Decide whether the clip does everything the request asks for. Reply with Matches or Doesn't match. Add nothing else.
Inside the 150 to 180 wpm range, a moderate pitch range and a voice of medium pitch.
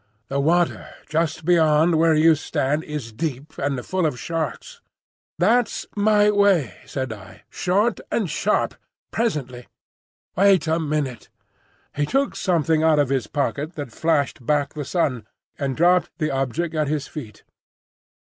Doesn't match